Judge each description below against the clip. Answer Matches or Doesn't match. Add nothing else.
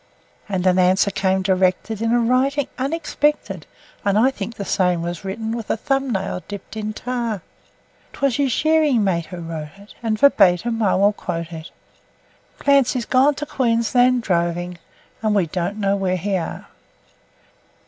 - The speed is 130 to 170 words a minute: Matches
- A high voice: Matches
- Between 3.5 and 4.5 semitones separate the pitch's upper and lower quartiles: Doesn't match